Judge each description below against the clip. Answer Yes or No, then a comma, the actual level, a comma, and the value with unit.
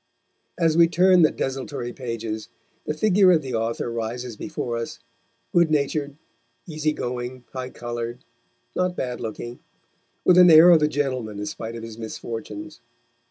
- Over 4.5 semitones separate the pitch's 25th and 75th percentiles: Yes, average, 5.2 semitones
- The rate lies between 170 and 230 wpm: No, average, 150 wpm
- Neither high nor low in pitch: No, low, 130 Hz